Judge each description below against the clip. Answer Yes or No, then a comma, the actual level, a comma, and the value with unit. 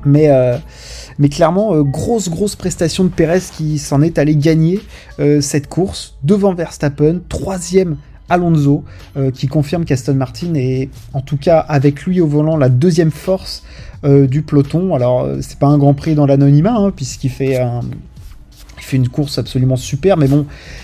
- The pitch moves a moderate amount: Yes, average, 3.5 semitones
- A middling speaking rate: Yes, average, 175 wpm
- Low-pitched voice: No, medium, 150 Hz